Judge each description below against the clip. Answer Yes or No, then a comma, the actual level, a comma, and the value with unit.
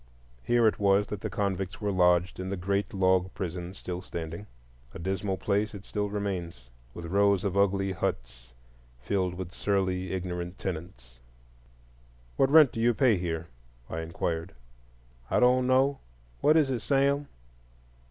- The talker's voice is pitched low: Yes, very low, 95 Hz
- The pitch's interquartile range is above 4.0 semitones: No, average, 2.9 semitones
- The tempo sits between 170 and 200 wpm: No, average, 150 wpm